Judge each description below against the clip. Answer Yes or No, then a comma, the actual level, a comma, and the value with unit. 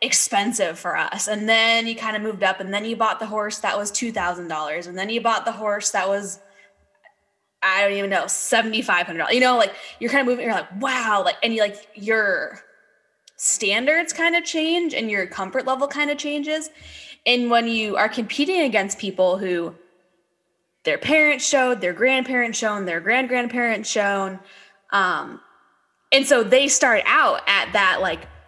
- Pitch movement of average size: Yes, average, 4.7 semitones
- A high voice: Yes, high, 220 Hz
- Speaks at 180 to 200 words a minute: Yes, average, 190 wpm